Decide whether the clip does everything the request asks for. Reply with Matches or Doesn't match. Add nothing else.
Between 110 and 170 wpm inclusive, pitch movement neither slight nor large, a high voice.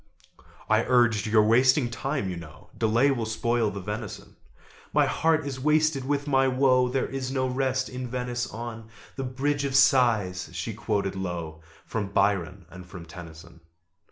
Doesn't match